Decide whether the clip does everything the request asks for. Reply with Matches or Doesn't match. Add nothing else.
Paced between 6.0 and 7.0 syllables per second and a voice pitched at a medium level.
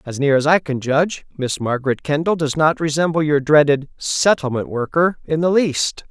Doesn't match